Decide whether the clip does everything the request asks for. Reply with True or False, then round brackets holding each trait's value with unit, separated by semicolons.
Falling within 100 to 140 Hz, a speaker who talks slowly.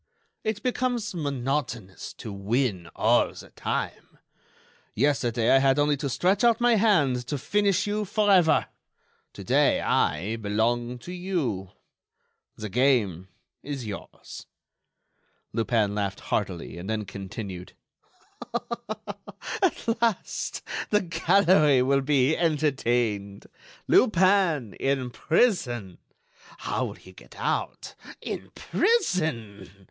True (135 Hz; 105 wpm)